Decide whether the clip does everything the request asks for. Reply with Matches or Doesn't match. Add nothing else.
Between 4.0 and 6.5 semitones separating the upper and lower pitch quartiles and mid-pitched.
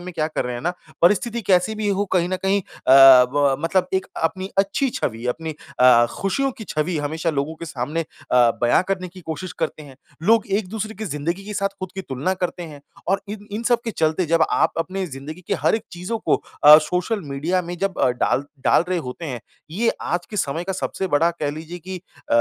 Matches